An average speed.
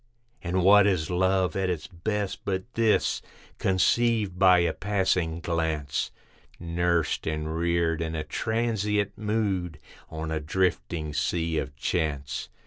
No: slow, 130 wpm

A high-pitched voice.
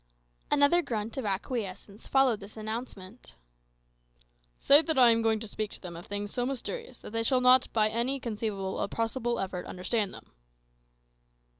Yes: high, 225 Hz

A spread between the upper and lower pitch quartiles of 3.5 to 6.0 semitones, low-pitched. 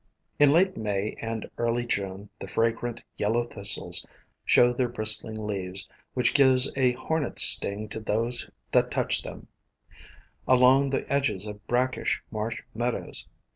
No: average, 3.1 semitones; low, 115 Hz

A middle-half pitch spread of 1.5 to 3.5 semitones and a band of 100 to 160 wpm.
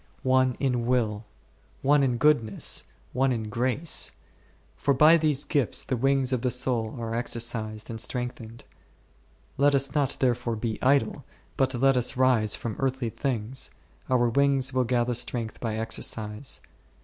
Yes: average, 2.7 semitones; average, 150 wpm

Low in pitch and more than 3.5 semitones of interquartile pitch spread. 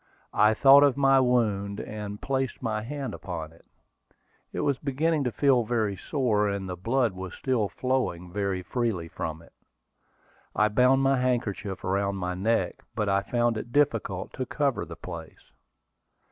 Yes: low, 110 Hz; average, 5.0 semitones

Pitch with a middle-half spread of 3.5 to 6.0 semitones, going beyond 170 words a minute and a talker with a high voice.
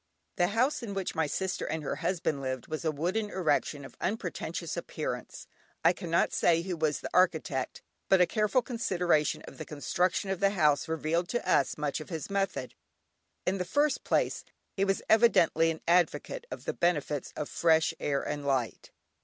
No: average, 4.3 semitones; average, 180 wpm; medium, 170 Hz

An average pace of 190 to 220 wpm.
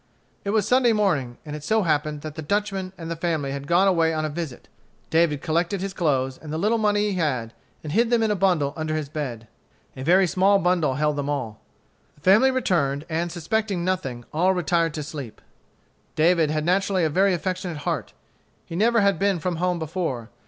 Yes: fast, 205 wpm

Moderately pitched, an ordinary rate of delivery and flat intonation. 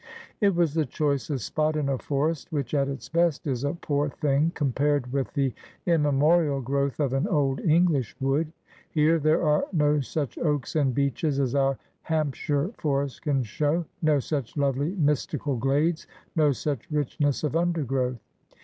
Yes: medium, 145 Hz; average, 170 wpm; narrow, 2.3 semitones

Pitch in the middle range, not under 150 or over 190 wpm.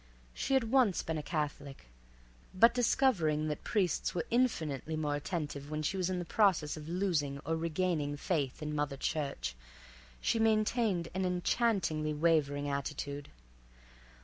No: medium, 160 Hz; average, 140 wpm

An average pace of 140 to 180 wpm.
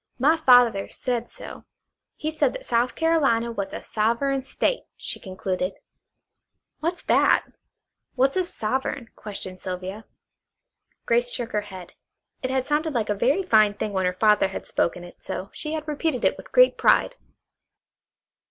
Yes: average, 155 wpm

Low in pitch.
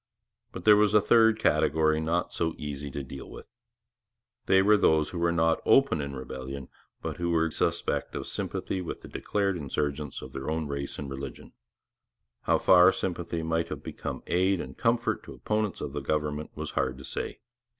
Yes: very low, 80 Hz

